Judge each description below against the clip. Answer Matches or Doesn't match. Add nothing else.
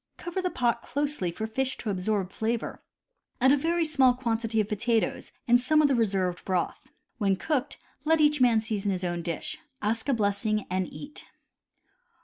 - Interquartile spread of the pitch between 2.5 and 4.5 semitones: Doesn't match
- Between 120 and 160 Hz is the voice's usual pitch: Doesn't match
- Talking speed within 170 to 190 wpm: Matches